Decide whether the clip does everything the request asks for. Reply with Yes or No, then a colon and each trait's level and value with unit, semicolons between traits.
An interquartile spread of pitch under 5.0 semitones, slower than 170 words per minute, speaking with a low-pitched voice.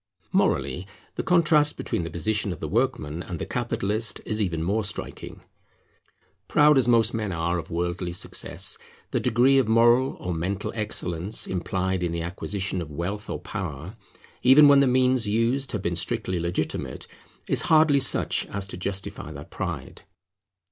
No: wide, 5.4 semitones; average, 160 wpm; low, 100 Hz